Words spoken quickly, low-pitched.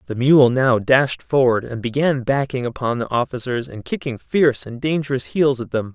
No: average, 190 wpm; low, 125 Hz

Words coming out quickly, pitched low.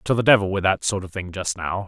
Yes: fast, 320 wpm; very low, 95 Hz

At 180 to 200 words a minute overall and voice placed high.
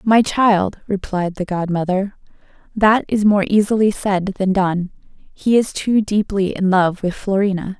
No: average, 155 wpm; high, 195 Hz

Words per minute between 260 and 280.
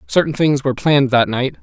No: fast, 220 wpm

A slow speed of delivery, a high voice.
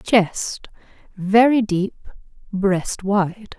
Yes: slow, 65 wpm; high, 200 Hz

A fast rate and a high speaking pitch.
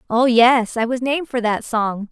Yes: fast, 225 wpm; high, 235 Hz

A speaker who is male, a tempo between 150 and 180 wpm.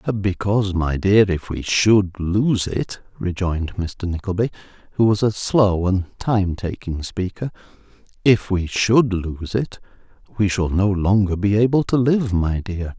Yes: male; average, 155 wpm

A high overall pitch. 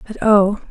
Yes: high, 205 Hz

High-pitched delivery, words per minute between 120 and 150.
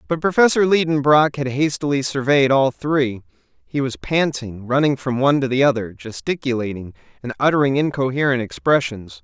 No: low, 135 Hz; average, 145 wpm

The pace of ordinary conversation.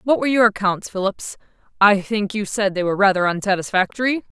Yes: average, 180 wpm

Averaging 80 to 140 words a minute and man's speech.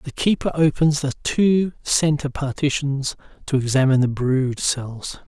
Yes: slow, 135 wpm; male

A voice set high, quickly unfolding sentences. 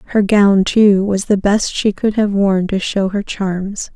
Yes: high, 200 Hz; fast, 215 wpm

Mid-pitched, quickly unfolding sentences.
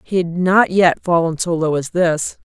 Yes: medium, 170 Hz; fast, 220 wpm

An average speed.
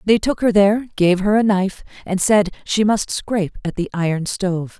No: fast, 215 wpm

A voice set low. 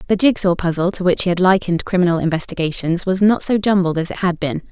No: medium, 180 Hz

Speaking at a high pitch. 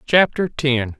No: medium, 140 Hz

